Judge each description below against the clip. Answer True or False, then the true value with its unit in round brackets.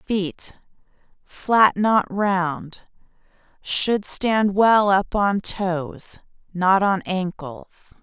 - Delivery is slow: True (90 wpm)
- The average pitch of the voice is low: False (195 Hz)